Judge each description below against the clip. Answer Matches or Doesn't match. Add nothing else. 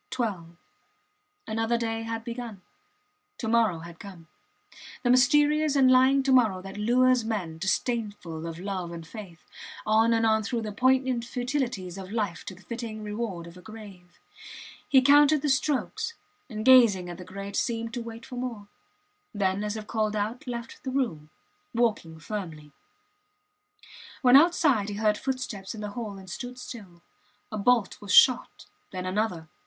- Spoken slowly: Doesn't match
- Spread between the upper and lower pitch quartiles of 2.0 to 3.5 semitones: Doesn't match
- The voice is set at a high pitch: Matches